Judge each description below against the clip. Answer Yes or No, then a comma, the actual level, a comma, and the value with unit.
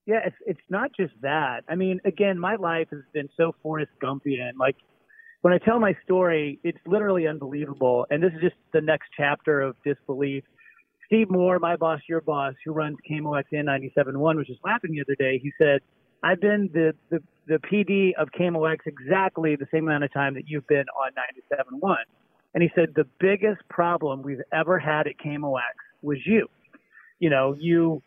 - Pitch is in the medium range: Yes, medium, 155 Hz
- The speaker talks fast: No, average, 195 wpm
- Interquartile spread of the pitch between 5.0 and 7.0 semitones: No, average, 4.4 semitones